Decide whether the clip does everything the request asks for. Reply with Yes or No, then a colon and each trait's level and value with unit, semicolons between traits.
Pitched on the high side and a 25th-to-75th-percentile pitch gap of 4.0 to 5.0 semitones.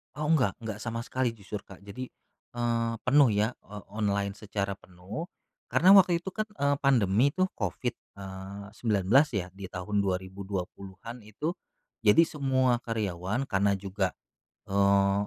No: low, 105 Hz; average, 4.7 semitones